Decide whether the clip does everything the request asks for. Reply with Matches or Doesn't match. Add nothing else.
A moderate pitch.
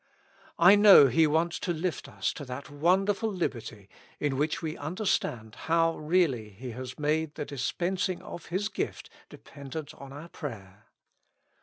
Matches